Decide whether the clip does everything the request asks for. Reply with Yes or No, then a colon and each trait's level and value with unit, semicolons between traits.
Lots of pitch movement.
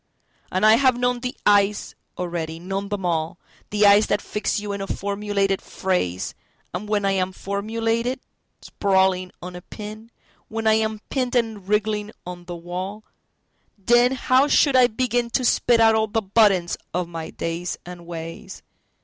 No: average, 3.5 semitones